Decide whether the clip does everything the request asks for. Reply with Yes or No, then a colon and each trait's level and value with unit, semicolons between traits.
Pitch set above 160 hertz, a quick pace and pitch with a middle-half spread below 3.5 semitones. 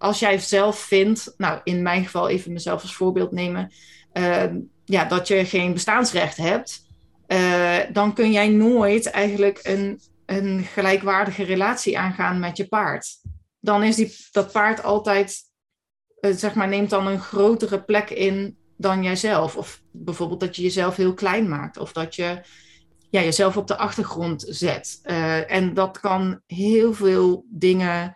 No: high, 190 Hz; average, 160 wpm; narrow, 2.5 semitones